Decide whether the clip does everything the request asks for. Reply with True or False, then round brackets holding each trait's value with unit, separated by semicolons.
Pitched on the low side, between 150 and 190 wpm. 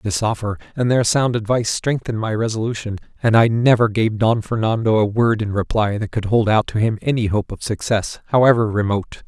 False (110 Hz; 200 wpm)